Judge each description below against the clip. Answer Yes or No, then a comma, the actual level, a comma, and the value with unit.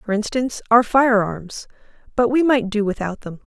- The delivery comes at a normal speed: Yes, average, 170 wpm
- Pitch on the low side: No, high, 225 Hz